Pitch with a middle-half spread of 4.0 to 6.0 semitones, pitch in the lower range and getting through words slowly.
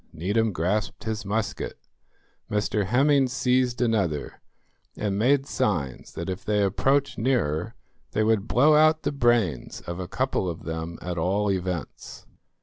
No: wide, 5.6 semitones; low, 105 Hz; average, 145 wpm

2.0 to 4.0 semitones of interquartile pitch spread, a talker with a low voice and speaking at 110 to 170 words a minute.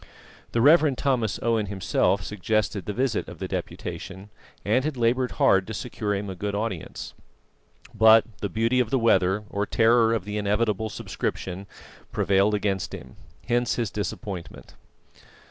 Yes: average, 2.7 semitones; low, 105 Hz; average, 150 wpm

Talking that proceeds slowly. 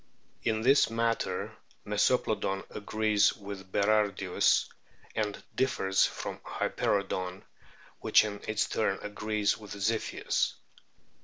Yes: slow, 100 wpm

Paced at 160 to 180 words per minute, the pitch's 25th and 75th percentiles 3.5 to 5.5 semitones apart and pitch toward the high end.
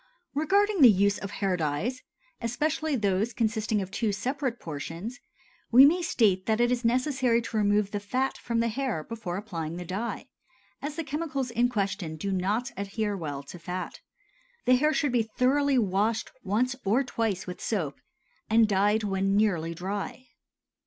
Yes: average, 165 wpm; average, 4.6 semitones; high, 220 Hz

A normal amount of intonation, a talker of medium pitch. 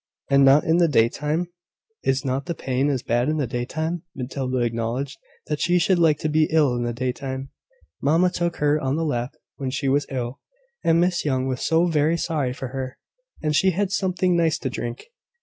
Yes: average, 4.0 semitones; medium, 145 Hz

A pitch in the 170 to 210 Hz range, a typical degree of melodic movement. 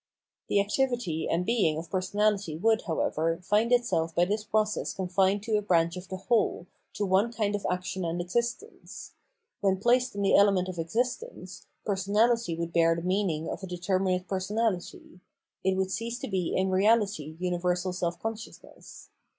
Yes: high, 190 Hz; average, 3.3 semitones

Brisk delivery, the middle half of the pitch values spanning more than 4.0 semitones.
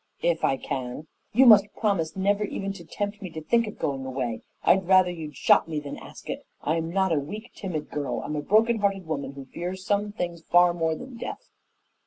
Yes: fast, 215 wpm; average, 4.9 semitones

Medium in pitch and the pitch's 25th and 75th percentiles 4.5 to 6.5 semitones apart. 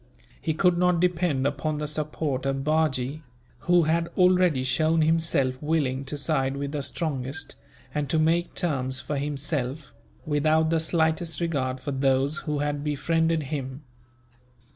No: medium, 150 Hz; average, 3.0 semitones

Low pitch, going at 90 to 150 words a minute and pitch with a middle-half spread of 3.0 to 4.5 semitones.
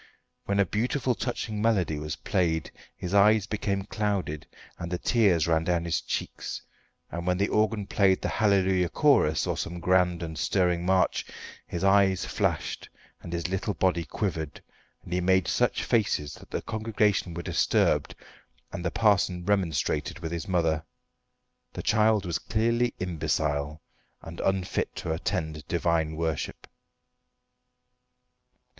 Yes: very low, 90 Hz; average, 140 wpm; average, 3.6 semitones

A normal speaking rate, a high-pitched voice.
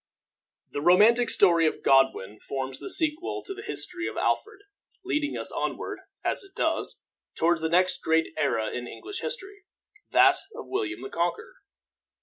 Yes: average, 155 wpm; high, 235 Hz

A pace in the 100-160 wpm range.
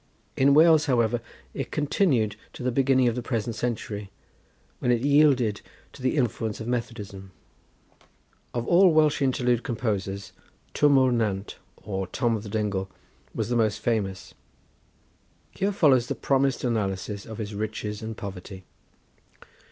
Yes: average, 145 wpm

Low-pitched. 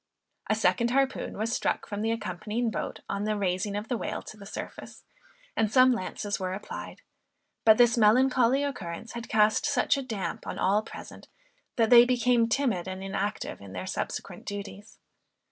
No: high, 220 Hz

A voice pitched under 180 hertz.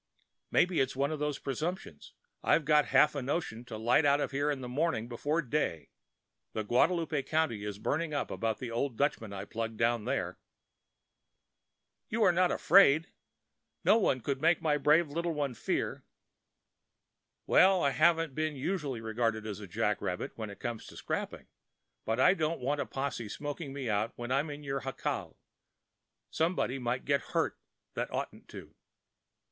Yes: medium, 140 Hz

